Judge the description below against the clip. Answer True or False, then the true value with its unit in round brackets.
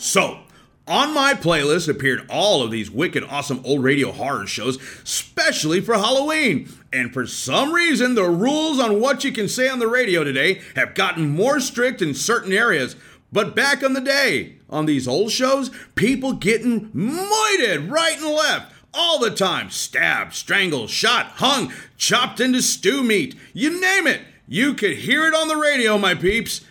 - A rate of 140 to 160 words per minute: False (175 wpm)